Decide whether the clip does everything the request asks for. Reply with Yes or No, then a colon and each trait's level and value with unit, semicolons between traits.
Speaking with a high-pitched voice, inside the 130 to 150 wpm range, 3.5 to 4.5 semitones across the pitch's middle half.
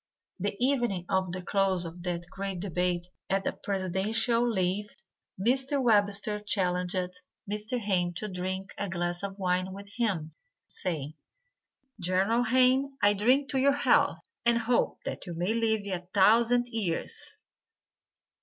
Yes: high, 195 Hz; average, 140 wpm; average, 4.0 semitones